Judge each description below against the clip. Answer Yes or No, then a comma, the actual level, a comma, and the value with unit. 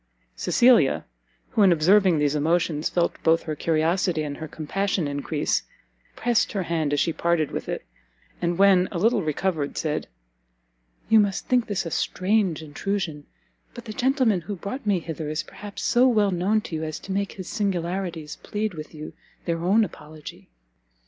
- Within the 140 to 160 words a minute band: No, average, 170 wpm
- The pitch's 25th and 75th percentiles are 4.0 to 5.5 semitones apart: Yes, average, 4.5 semitones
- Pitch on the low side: No, medium, 175 Hz